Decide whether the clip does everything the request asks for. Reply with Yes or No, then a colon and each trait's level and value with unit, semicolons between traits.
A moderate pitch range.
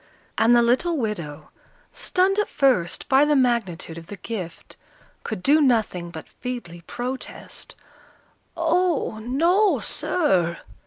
No: wide, 8.8 semitones